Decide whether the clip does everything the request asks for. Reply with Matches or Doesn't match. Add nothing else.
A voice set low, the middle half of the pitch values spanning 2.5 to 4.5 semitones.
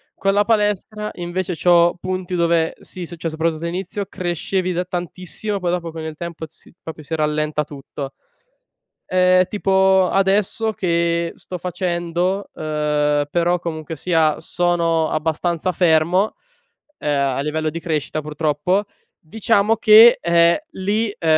Doesn't match